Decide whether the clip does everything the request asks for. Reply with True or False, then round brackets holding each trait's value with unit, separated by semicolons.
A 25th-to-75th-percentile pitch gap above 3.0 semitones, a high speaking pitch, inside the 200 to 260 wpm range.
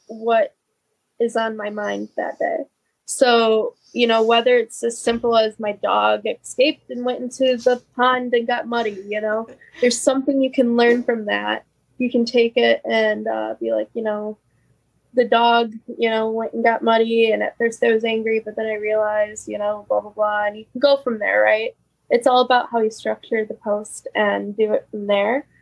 False (2.6 semitones; 225 Hz; 205 wpm)